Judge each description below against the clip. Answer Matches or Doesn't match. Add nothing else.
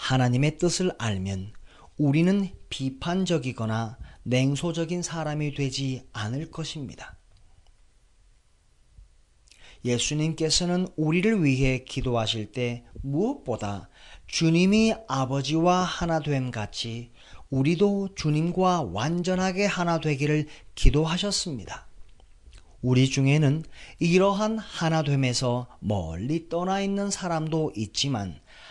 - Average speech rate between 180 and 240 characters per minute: Matches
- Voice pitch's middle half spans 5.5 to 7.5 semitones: Matches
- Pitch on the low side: Doesn't match